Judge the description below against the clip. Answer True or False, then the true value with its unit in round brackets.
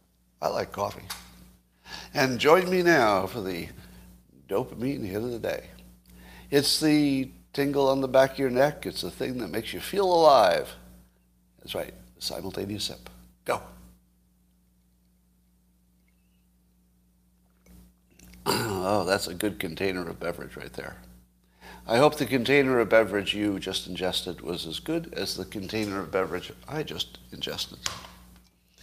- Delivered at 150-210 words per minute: False (135 wpm)